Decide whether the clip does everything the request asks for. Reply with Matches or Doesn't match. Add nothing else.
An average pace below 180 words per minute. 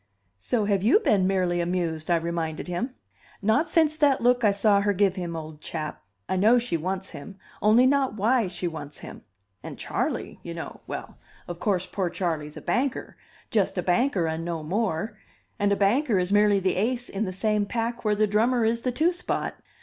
Doesn't match